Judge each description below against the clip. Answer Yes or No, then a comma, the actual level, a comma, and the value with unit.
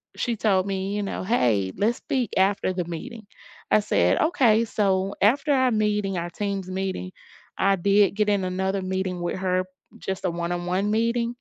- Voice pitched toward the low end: No, high, 195 Hz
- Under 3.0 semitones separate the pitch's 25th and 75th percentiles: Yes, narrow, 2.5 semitones